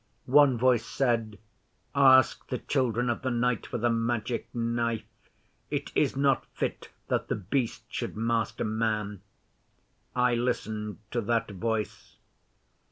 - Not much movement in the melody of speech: Yes, narrow, 2.1 semitones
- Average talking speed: No, slow, 130 wpm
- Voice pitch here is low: Yes, low, 115 Hz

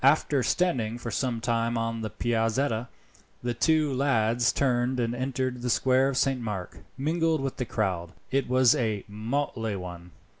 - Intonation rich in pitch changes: No, average, 3.0 semitones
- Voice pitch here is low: Yes, low, 120 Hz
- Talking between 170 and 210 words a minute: No, average, 160 wpm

